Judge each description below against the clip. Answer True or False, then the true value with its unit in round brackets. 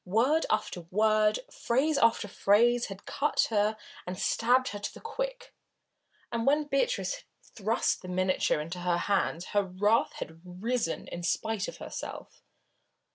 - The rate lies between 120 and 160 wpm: True (150 wpm)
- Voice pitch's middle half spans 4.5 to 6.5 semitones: True (5.1 semitones)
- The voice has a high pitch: True (215 Hz)